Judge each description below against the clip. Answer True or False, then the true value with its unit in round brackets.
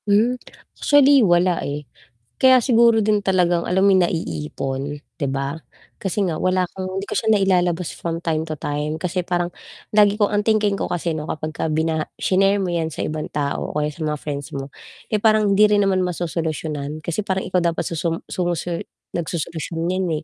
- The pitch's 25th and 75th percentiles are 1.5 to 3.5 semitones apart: False (4.0 semitones)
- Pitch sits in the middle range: True (175 Hz)